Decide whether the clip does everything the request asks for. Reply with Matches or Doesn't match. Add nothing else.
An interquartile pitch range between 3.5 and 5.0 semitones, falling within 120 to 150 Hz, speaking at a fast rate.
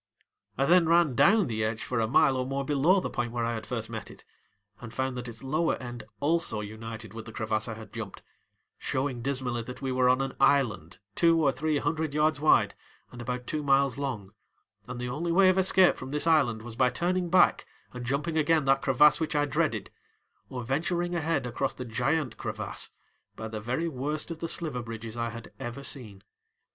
Matches